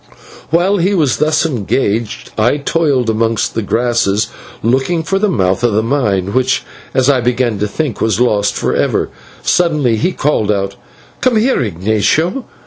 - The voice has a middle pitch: No, low, 125 Hz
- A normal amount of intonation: No, wide, 6.3 semitones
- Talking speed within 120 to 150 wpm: No, average, 160 wpm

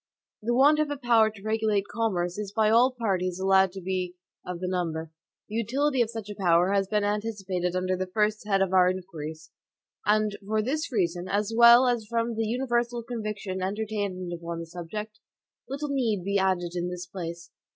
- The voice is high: Yes, high, 205 Hz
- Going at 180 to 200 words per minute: Yes, average, 190 wpm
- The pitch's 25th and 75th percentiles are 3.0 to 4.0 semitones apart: Yes, average, 3.7 semitones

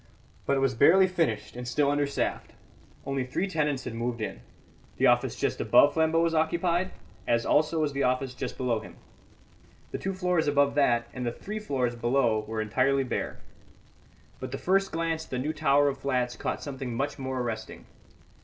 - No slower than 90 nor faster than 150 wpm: No, average, 185 wpm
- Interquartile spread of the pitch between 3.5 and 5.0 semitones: Yes, average, 4.4 semitones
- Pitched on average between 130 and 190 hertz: Yes, medium, 140 Hz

